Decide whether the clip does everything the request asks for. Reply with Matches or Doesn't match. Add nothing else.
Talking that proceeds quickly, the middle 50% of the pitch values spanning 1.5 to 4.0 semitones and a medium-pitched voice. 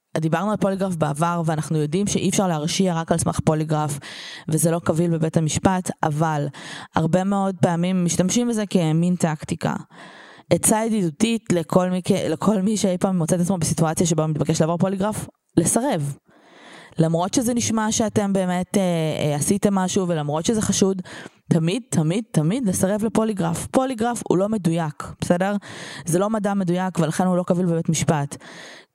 Matches